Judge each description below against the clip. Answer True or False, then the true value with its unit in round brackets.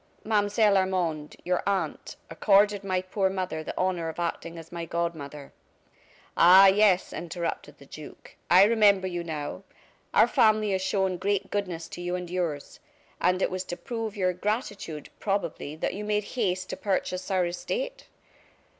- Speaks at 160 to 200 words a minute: True (165 wpm)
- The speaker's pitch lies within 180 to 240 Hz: True (185 Hz)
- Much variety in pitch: False (2.9 semitones)